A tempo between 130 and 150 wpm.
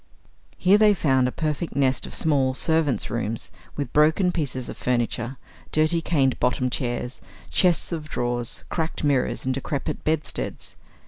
Yes: average, 145 wpm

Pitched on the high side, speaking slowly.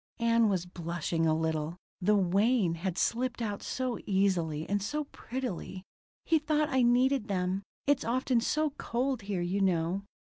No: high, 200 Hz; average, 155 wpm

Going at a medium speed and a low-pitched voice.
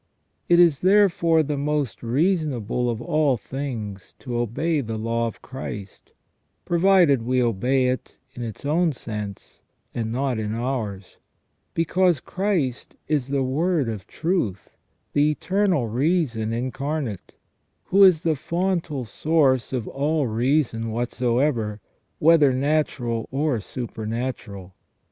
No: slow, 120 wpm; low, 130 Hz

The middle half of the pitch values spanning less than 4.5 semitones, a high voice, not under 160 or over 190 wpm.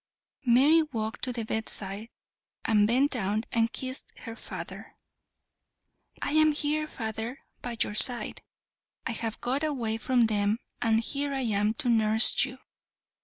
No: average, 3.4 semitones; high, 235 Hz; average, 145 wpm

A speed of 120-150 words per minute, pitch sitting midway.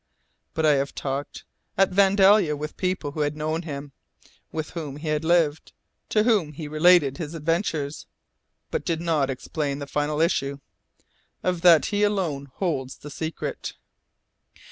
Yes: average, 145 wpm; medium, 155 Hz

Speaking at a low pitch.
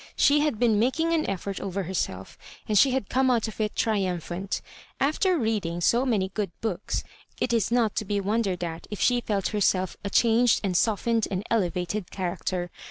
No: high, 210 Hz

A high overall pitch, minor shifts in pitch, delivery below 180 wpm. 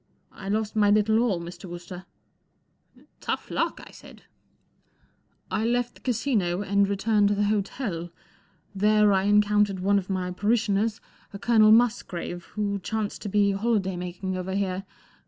Yes: high, 205 Hz; narrow, 2.2 semitones; average, 160 wpm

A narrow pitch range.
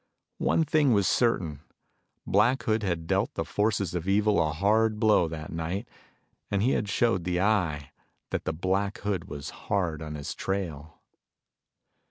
No: average, 4.7 semitones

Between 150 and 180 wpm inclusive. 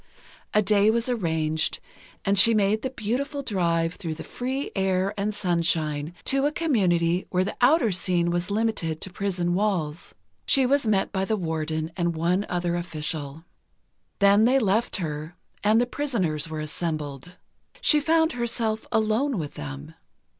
Yes: average, 155 wpm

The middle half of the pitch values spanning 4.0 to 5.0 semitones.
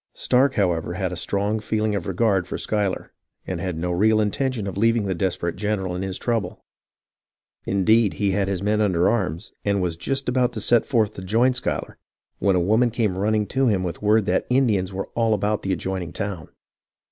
No: average, 3.0 semitones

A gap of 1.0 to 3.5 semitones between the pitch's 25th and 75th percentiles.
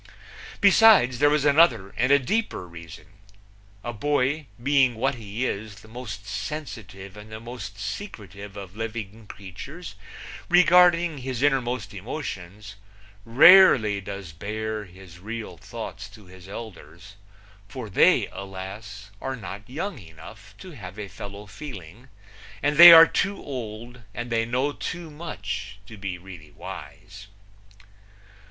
No: wide, 5.5 semitones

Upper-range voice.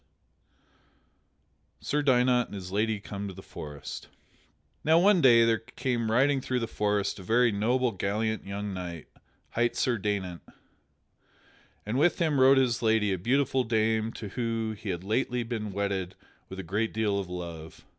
No: low, 110 Hz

